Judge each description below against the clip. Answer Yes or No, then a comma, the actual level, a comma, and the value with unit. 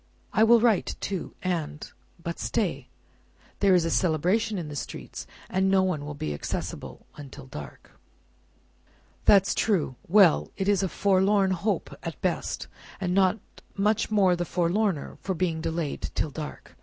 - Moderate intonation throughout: Yes, average, 3.7 semitones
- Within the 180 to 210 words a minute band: No, average, 155 wpm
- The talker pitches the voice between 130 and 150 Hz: No, medium, 185 Hz